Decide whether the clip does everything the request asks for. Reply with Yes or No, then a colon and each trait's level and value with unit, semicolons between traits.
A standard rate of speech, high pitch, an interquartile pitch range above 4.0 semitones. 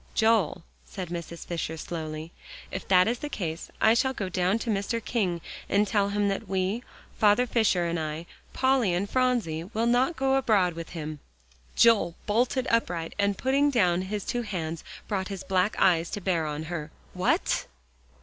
Yes: average, 175 wpm; high, 195 Hz; average, 5.1 semitones